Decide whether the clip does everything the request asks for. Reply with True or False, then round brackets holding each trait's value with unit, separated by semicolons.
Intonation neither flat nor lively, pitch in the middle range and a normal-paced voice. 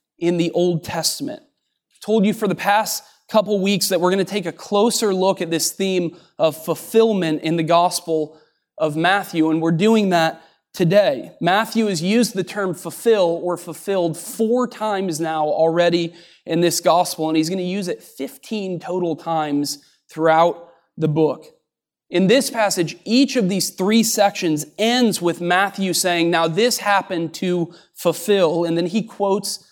True (3.8 semitones; 180 Hz; 170 wpm)